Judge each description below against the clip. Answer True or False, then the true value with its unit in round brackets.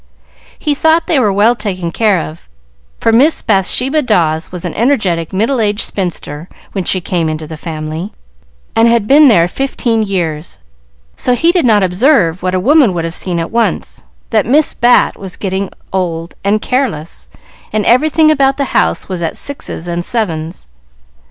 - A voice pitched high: True (200 Hz)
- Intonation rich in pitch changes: True (6.4 semitones)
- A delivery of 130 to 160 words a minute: False (170 wpm)